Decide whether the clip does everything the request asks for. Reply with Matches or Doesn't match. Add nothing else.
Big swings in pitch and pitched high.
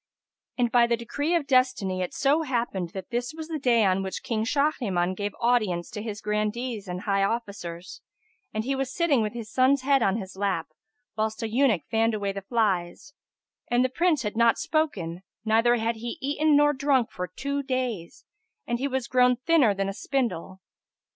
Doesn't match